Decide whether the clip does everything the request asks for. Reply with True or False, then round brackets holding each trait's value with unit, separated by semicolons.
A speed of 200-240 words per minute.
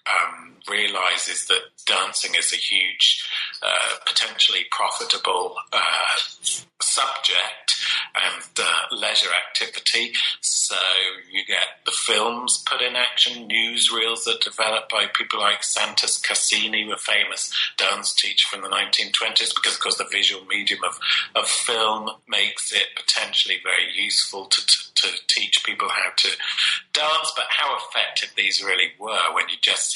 False (140 wpm)